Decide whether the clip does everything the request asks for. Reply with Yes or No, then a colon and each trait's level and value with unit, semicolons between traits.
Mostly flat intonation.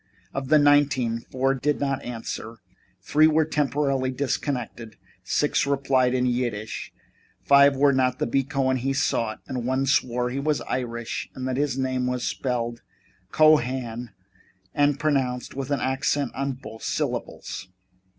Yes: narrow, 2.2 semitones